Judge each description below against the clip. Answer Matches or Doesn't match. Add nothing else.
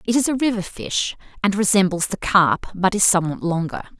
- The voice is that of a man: Doesn't match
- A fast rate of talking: Doesn't match